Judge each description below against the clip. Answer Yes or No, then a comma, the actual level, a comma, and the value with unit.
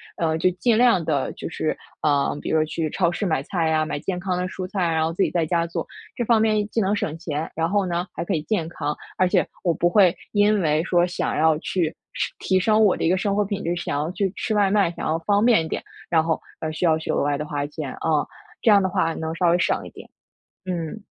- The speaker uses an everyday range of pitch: Yes, average, 3.7 semitones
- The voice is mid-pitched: Yes, medium, 175 Hz